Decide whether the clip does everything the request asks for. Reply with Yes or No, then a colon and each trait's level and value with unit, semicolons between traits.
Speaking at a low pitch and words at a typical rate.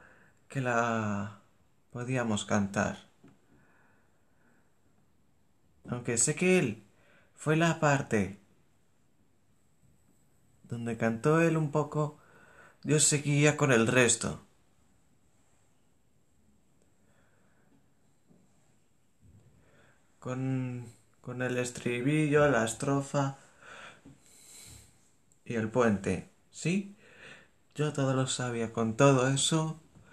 No: low, 125 Hz; slow, 75 wpm